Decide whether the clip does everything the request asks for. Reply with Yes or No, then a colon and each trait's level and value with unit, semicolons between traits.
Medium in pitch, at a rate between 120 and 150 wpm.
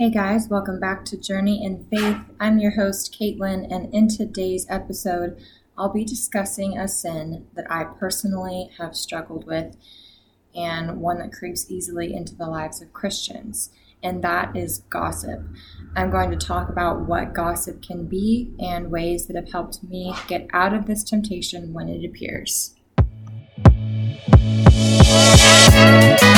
Yes: medium, 175 Hz; average, 145 wpm